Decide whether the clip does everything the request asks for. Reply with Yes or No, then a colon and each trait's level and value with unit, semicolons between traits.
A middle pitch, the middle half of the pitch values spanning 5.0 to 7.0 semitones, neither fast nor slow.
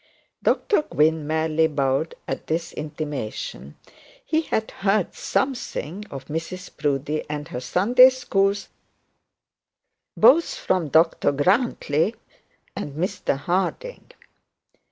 No: medium, 165 Hz; wide, 5.4 semitones; slow, 95 wpm